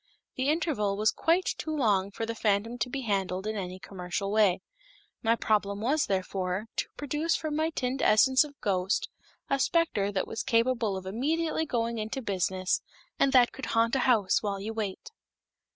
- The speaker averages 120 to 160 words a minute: No, average, 180 wpm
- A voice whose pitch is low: No, high, 225 Hz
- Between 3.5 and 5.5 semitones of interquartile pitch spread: Yes, average, 5.2 semitones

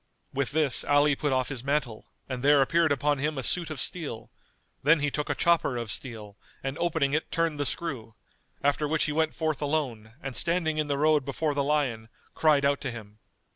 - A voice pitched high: No, medium, 145 Hz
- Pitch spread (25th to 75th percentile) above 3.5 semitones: No, average, 2.9 semitones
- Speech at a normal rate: No, fast, 210 wpm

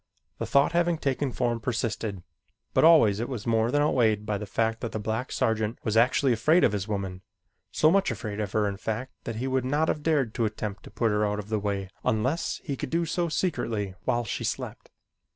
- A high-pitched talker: No, low, 115 Hz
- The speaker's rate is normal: No, fast, 225 wpm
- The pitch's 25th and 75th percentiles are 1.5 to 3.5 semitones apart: No, average, 4.3 semitones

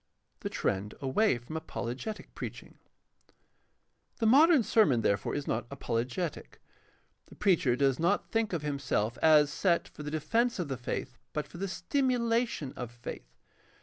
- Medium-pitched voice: Yes, medium, 150 Hz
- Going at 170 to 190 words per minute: No, average, 150 wpm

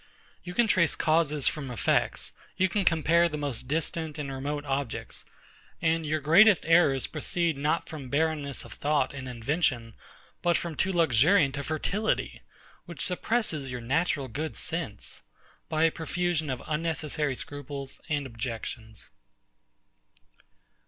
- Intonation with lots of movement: No, average, 3.4 semitones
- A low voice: No, medium, 150 Hz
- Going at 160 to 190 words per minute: No, slow, 135 wpm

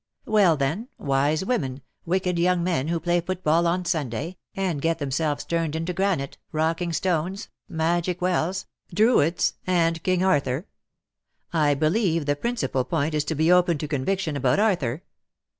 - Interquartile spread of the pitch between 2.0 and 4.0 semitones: Yes, average, 3.4 semitones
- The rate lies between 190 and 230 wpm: No, average, 175 wpm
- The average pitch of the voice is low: No, medium, 165 Hz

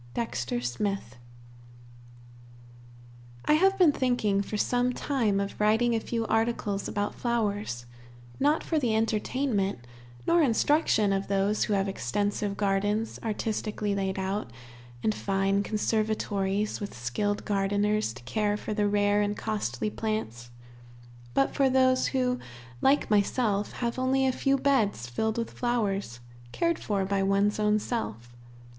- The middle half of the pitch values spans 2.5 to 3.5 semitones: Yes, average, 3.2 semitones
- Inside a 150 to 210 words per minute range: No, slow, 135 wpm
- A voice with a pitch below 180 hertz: No, high, 210 Hz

